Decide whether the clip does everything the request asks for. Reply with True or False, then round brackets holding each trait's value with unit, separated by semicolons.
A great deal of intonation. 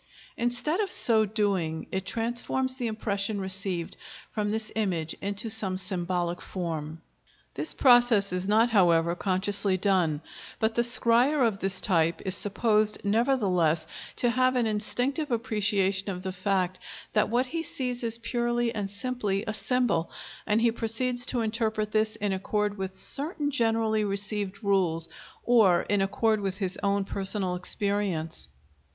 False (3.5 semitones)